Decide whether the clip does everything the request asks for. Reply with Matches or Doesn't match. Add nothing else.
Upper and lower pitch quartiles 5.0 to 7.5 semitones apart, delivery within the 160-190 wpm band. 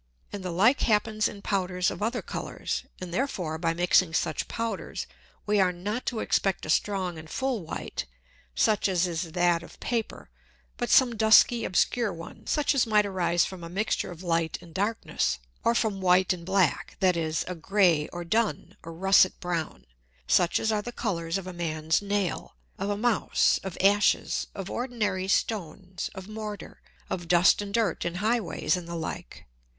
Doesn't match